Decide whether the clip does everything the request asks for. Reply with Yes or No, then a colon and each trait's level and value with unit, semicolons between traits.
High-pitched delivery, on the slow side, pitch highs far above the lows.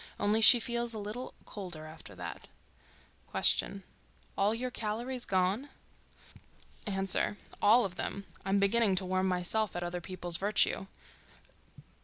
No: high, 200 Hz; slow, 120 wpm; average, 3.5 semitones